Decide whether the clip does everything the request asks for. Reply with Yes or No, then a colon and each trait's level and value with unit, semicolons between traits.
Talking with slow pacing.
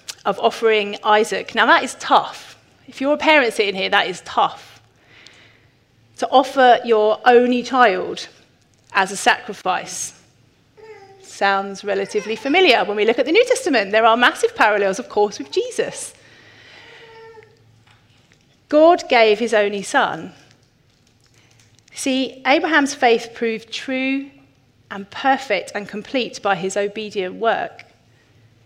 Yes: slow, 125 wpm